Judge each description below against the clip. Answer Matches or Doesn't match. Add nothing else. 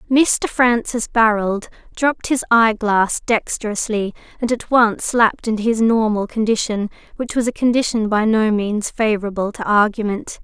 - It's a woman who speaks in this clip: Matches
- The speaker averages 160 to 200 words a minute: Doesn't match